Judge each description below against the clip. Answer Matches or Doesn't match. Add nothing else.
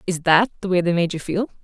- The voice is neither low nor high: Matches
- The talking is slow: Doesn't match